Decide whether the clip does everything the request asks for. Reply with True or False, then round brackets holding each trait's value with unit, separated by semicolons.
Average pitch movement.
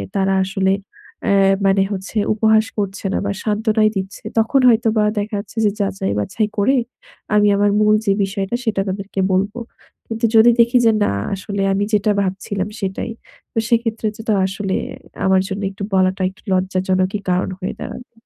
False (2.2 semitones)